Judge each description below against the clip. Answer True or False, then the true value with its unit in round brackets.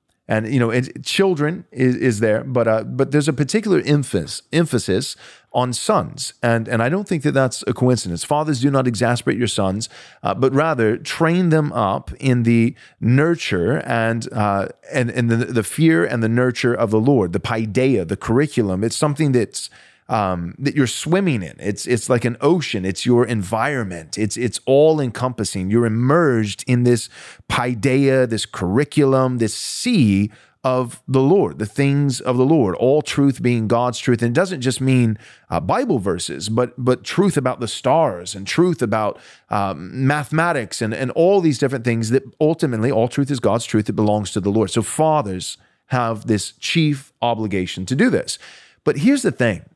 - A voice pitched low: True (125 Hz)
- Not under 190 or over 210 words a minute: False (180 wpm)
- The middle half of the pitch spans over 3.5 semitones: True (4.2 semitones)